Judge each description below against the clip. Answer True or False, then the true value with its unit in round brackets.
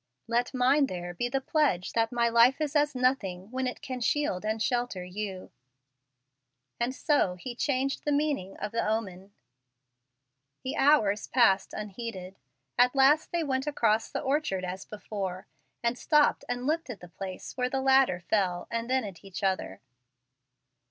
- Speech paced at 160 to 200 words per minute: True (165 wpm)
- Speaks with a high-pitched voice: True (235 Hz)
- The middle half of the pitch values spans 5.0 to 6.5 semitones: True (5.5 semitones)